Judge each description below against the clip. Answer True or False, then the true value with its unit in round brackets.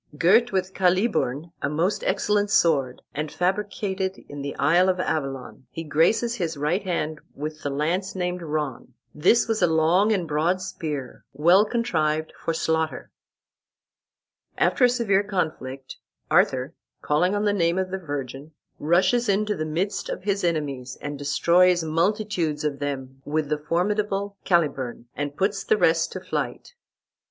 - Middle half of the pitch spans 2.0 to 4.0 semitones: False (4.6 semitones)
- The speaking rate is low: False (150 wpm)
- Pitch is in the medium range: True (170 Hz)